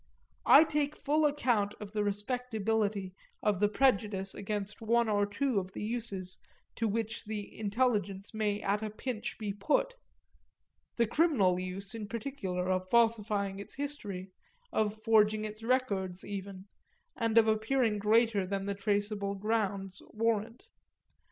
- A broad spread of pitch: No, narrow, 2.4 semitones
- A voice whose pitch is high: Yes, high, 210 Hz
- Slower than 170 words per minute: Yes, average, 140 wpm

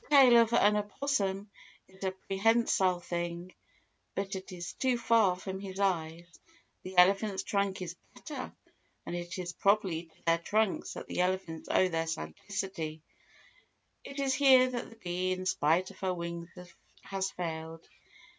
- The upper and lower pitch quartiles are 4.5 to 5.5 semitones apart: No, average, 3.3 semitones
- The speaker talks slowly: No, average, 155 wpm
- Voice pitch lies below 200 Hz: Yes, high, 190 Hz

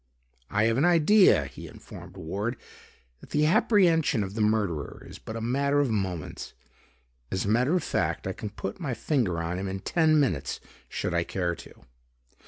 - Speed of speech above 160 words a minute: Yes, average, 185 wpm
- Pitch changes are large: Yes, wide, 7.6 semitones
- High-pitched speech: No, low, 115 Hz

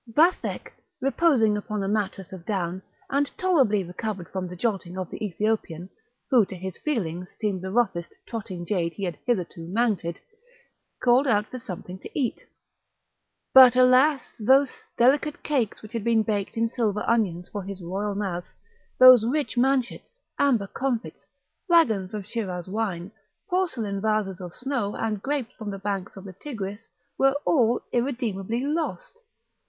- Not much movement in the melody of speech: No, average, 4.9 semitones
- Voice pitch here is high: Yes, high, 215 Hz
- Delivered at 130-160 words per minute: Yes, average, 155 wpm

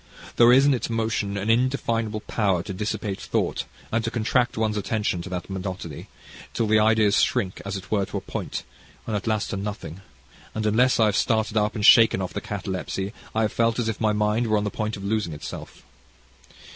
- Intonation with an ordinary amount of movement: No, narrow, 2.2 semitones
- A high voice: No, low, 105 Hz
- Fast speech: Yes, fast, 210 wpm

